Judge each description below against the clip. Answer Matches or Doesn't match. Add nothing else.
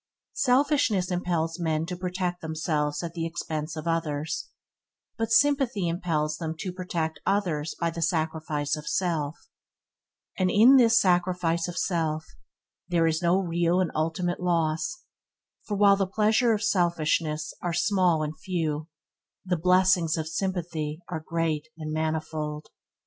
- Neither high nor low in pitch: Matches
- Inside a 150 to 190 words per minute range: Doesn't match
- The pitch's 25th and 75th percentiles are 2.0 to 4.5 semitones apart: Matches